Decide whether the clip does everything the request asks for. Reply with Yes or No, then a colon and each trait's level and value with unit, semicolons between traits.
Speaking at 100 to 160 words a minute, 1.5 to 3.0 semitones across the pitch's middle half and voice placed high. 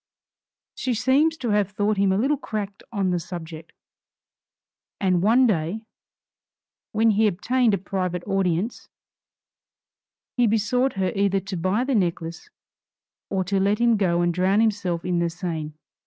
No: average, 150 wpm; average, 3.7 semitones; high, 195 Hz